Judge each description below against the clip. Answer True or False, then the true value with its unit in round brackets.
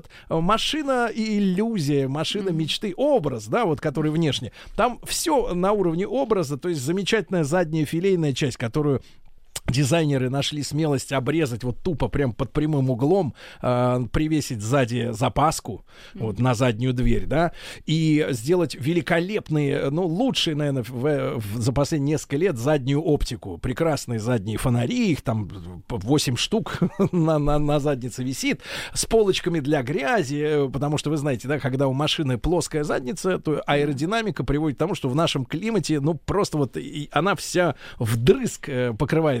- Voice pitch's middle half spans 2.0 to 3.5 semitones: False (4.2 semitones)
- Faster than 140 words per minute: True (150 wpm)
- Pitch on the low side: False (150 Hz)